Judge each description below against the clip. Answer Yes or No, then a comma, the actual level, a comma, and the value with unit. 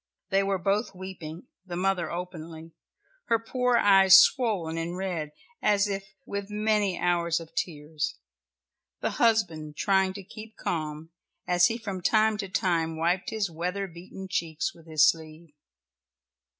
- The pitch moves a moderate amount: Yes, average, 3.3 semitones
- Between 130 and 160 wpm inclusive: Yes, average, 145 wpm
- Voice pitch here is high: No, medium, 180 Hz